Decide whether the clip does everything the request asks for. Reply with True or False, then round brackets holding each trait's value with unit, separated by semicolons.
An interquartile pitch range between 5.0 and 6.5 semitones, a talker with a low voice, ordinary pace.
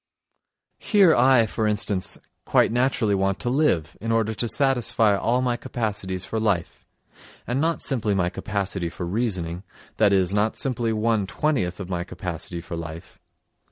False (4.5 semitones; 105 Hz; 160 wpm)